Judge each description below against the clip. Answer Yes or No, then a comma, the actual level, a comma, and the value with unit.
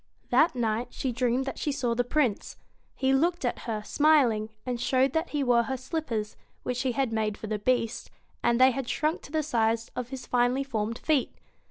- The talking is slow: No, fast, 205 wpm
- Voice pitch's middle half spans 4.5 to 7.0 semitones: No, average, 2.9 semitones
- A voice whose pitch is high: Yes, very high, 250 Hz